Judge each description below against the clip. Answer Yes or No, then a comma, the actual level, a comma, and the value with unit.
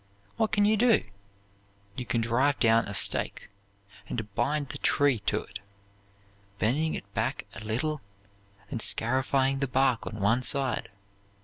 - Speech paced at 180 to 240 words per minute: No, average, 145 wpm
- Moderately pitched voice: No, low, 130 Hz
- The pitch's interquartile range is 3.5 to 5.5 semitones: Yes, average, 4.1 semitones